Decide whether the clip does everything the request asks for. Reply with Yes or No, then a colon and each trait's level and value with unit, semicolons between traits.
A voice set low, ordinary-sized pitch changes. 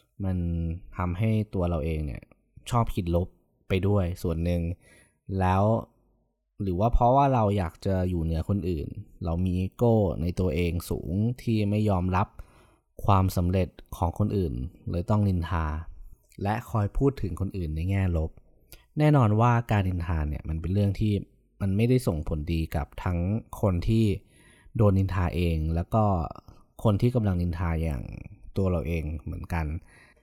Yes: very low, 90 Hz; average, 3.7 semitones